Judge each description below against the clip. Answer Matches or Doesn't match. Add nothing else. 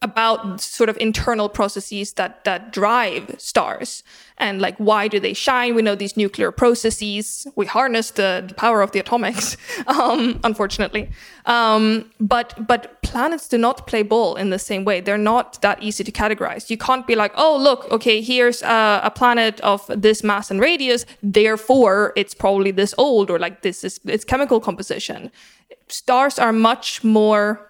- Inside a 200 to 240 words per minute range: Doesn't match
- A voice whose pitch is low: Doesn't match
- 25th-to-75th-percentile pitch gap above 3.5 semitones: Doesn't match